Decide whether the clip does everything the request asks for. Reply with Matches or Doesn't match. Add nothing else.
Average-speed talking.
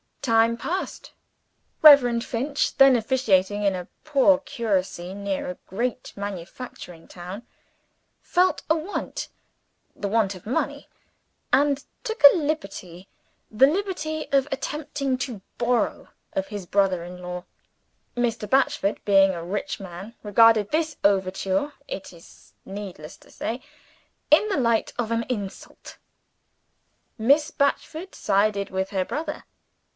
Doesn't match